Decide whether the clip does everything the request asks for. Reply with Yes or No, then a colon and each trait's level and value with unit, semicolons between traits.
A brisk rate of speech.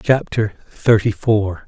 No: slow, 110 wpm